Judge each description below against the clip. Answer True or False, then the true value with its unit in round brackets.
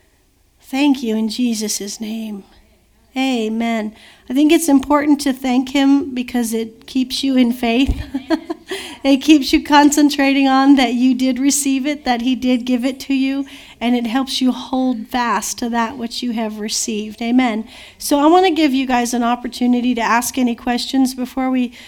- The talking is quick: False (175 wpm)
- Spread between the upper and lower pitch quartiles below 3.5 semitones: True (2.6 semitones)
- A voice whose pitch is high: True (255 Hz)